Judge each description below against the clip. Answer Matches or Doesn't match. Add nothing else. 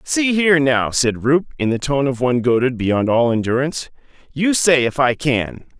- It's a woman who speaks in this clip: Doesn't match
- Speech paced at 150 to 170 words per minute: Doesn't match